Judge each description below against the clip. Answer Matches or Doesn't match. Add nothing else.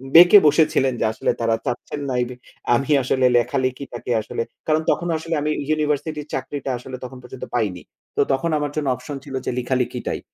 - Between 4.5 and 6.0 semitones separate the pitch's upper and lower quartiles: Doesn't match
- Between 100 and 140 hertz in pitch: Matches